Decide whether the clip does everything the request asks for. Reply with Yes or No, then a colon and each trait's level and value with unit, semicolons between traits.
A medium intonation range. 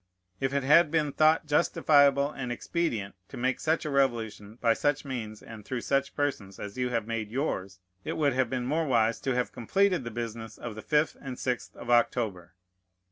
Yes: average, 4.2 semitones